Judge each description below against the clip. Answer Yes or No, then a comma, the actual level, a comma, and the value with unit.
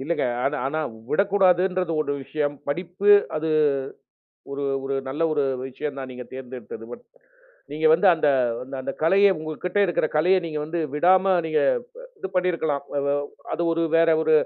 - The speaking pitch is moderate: Yes, medium, 160 Hz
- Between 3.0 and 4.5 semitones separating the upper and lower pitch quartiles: Yes, average, 4.1 semitones